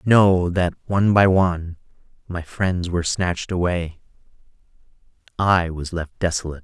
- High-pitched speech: No, very low, 90 Hz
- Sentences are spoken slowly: Yes, slow, 125 wpm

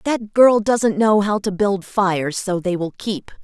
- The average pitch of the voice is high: Yes, high, 200 Hz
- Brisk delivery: Yes, fast, 210 wpm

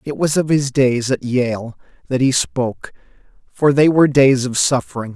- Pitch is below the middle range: Yes, low, 130 Hz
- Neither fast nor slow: Yes, average, 185 wpm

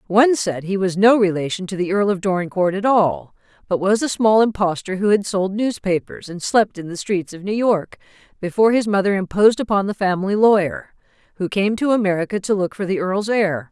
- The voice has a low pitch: No, high, 195 Hz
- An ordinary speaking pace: No, fast, 210 wpm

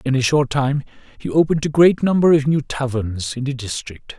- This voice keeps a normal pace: No, fast, 215 wpm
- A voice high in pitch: No, low, 135 Hz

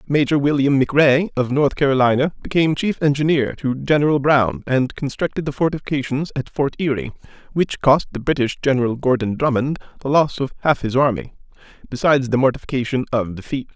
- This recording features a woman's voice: No, male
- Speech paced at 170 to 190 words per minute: No, average, 160 wpm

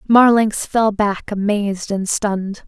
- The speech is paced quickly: No, slow, 135 wpm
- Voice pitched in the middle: No, high, 205 Hz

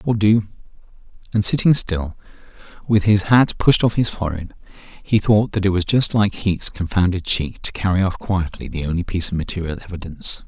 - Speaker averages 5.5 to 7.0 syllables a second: Yes, 5.6 syllables/s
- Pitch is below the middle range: Yes, very low, 95 Hz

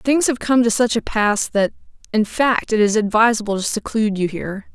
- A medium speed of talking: No, fast, 215 wpm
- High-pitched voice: Yes, high, 220 Hz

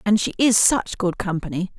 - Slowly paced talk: No, average, 200 wpm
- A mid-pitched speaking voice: No, high, 200 Hz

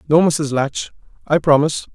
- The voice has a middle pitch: Yes, medium, 150 Hz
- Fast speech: No, average, 155 wpm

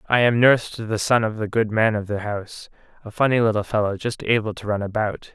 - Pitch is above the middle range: No, low, 110 Hz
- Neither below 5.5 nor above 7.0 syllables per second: Yes, 6.0 syllables/s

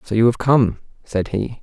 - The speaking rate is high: Yes, fast, 220 wpm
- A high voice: No, low, 115 Hz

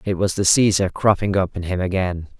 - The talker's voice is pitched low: Yes, very low, 95 Hz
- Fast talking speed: Yes, fast, 225 wpm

